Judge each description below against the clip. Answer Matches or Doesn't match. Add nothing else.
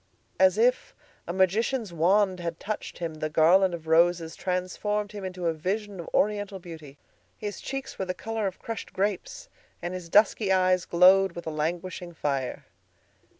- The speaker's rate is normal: Matches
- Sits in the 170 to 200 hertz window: Matches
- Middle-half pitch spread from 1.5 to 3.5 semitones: Matches